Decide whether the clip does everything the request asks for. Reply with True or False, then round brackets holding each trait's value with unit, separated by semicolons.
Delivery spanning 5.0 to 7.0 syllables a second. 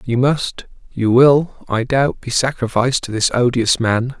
False (4.4 syllables/s)